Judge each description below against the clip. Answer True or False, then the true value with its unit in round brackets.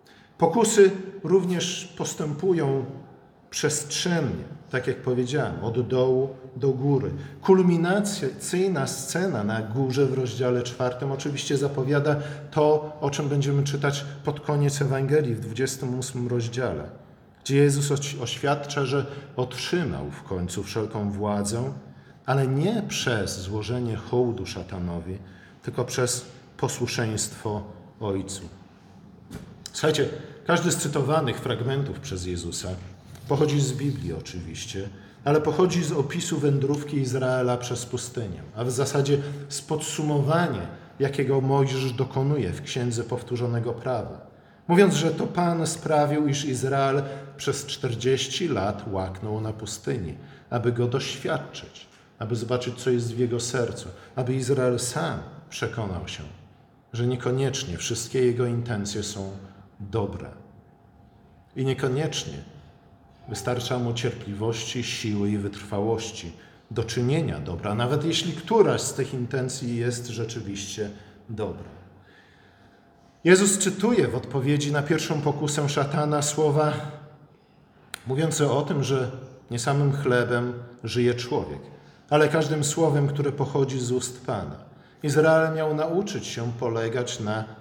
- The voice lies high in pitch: False (130 Hz)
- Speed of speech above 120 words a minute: False (115 wpm)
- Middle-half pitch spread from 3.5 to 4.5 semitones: True (4.2 semitones)